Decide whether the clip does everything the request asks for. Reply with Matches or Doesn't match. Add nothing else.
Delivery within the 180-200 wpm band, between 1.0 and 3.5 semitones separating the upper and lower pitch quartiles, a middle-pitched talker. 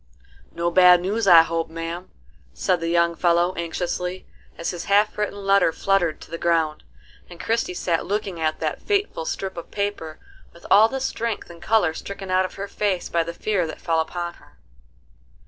Matches